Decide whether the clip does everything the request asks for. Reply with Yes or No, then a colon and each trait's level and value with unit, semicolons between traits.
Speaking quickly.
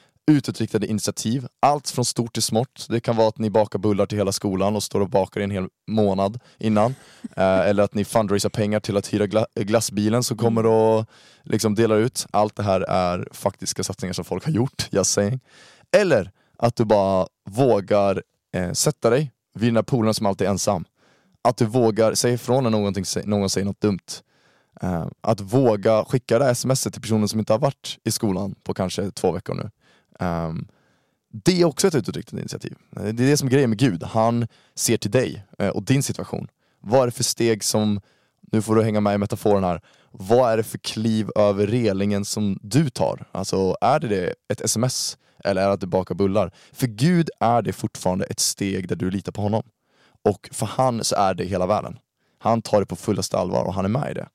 Yes: fast, 205 wpm